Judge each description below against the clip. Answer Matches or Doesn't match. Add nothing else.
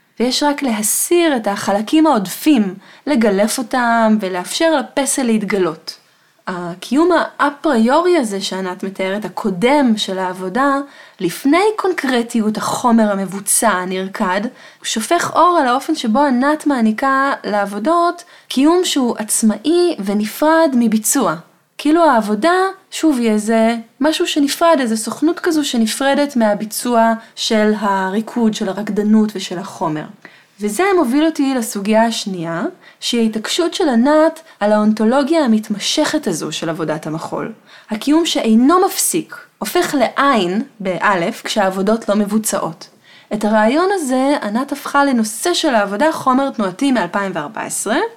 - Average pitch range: Doesn't match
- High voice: Matches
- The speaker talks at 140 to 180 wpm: Doesn't match